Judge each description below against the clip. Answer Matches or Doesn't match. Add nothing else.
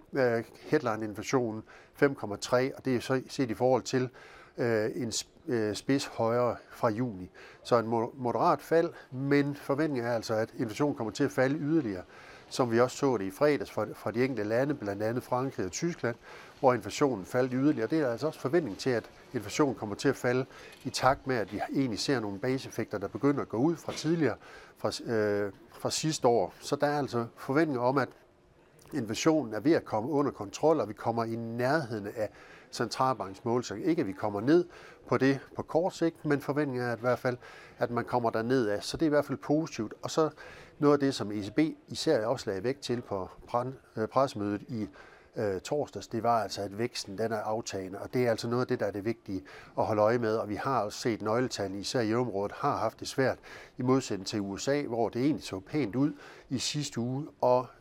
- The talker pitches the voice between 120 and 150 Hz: Matches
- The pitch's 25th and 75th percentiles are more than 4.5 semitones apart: Doesn't match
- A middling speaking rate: Matches